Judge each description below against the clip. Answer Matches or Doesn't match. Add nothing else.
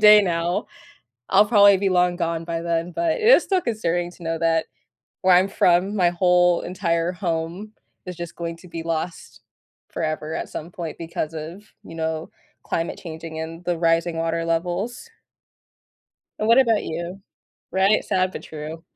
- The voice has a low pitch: Doesn't match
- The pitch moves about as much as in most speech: Doesn't match